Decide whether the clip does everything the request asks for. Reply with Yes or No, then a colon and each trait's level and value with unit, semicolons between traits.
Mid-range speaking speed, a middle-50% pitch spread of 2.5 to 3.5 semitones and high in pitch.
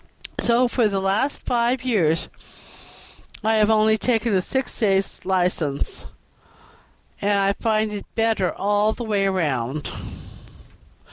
No: slow, 125 wpm; average, 2.9 semitones; high, 210 Hz